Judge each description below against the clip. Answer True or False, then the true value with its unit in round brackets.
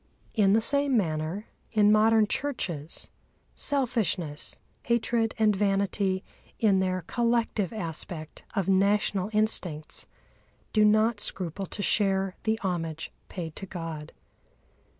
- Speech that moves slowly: True (110 wpm)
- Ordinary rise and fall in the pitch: True (3.7 semitones)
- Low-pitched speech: False (200 Hz)